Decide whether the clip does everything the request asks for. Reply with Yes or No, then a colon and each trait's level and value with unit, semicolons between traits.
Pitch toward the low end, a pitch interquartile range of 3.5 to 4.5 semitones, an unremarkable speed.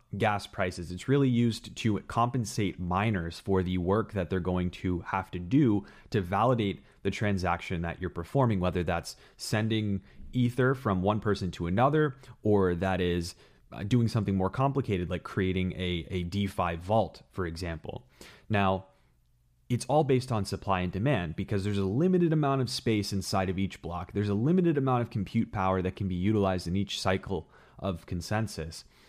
Yes: low, 100 Hz; average, 3.9 semitones; average, 175 wpm